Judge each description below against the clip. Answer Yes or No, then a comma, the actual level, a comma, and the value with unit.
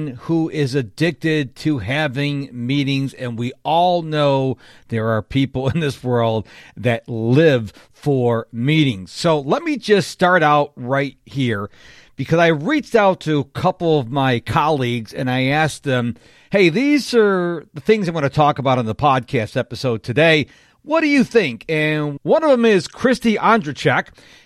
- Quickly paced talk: No, average, 165 wpm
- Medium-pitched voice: Yes, medium, 145 Hz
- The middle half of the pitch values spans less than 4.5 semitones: No, average, 4.8 semitones